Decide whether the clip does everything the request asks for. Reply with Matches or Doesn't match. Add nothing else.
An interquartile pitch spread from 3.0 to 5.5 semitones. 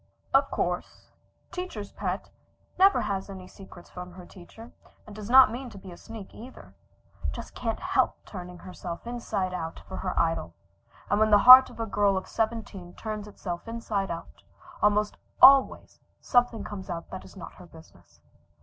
Matches